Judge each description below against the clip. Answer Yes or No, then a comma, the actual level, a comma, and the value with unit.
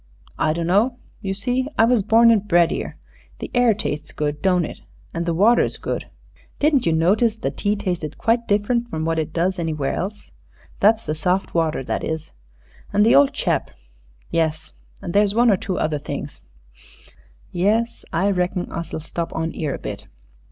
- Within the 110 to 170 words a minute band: No, average, 180 wpm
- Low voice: No, medium, 185 Hz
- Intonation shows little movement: No, average, 5.2 semitones